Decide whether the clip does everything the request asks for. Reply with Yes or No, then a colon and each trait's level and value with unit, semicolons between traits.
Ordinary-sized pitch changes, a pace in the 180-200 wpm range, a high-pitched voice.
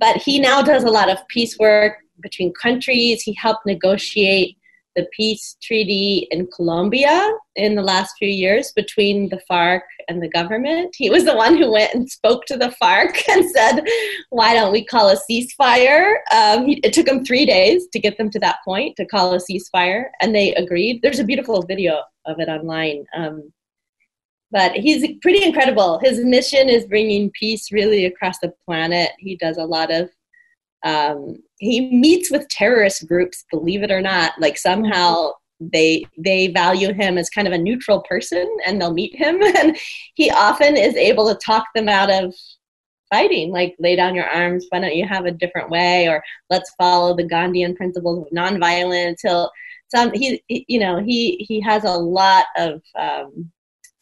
No: wide, 5.9 semitones; average, 185 wpm; high, 205 Hz